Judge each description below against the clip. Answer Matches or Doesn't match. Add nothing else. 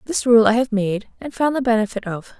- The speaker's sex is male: Doesn't match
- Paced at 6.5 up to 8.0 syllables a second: Doesn't match